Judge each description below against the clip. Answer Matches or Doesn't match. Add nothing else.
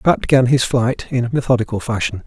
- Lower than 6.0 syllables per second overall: Matches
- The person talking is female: Doesn't match